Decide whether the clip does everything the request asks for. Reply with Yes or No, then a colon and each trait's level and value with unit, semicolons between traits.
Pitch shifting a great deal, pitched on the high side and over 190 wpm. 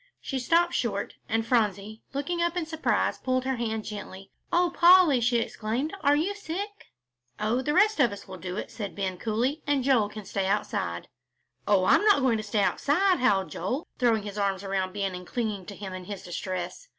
Yes: wide, 6.5 semitones; high, 225 Hz; average, 200 wpm